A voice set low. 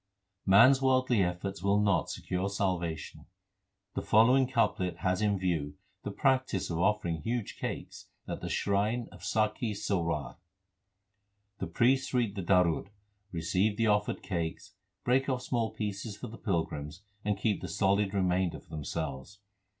Yes: low, 100 Hz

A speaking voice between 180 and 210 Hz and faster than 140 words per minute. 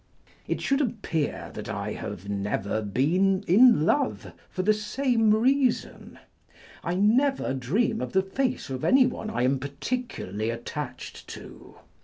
No: high, 190 Hz; slow, 135 wpm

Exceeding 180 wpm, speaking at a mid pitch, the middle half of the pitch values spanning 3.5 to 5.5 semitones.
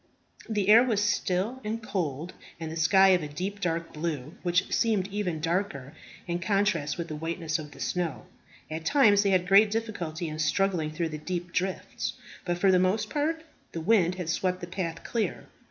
Yes: average, 190 wpm; medium, 180 Hz; average, 3.8 semitones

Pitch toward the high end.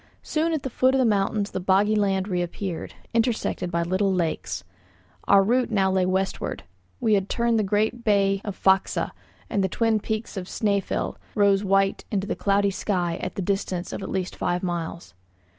Yes: high, 195 Hz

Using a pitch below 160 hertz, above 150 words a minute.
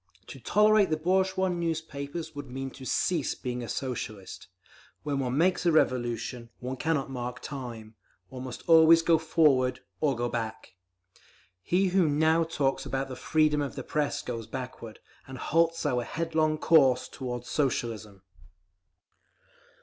No: medium, 140 Hz; average, 140 wpm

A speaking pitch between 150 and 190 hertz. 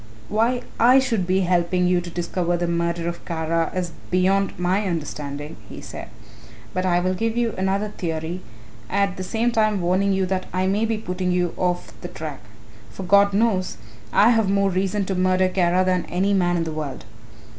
Yes: medium, 185 Hz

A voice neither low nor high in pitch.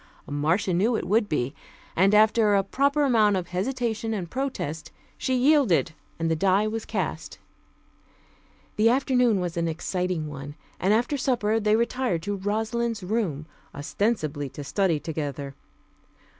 No: high, 205 Hz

